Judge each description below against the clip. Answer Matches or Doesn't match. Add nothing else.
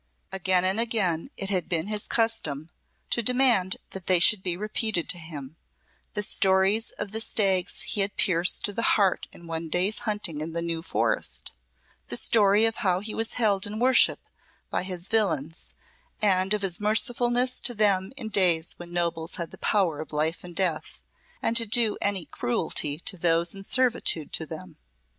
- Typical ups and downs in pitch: Matches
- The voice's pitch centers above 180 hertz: Matches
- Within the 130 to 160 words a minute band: Doesn't match